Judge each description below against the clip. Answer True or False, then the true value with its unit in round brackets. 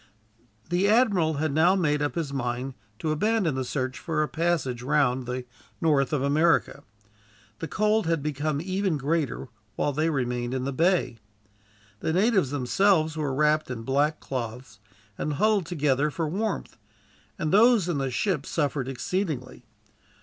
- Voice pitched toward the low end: False (150 Hz)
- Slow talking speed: False (155 wpm)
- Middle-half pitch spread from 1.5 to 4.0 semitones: False (4.4 semitones)